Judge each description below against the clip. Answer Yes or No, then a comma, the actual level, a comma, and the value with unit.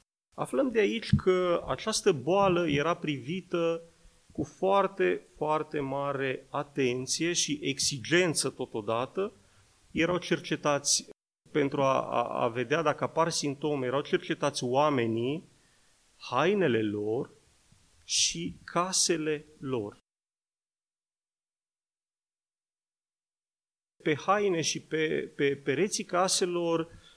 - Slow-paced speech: Yes, slow, 90 wpm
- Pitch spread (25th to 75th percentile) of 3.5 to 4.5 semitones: Yes, average, 4.1 semitones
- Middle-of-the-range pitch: Yes, medium, 155 Hz